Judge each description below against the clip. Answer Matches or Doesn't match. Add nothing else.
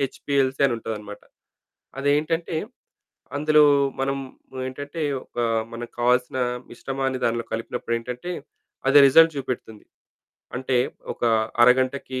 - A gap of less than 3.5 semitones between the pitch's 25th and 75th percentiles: Matches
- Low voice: Matches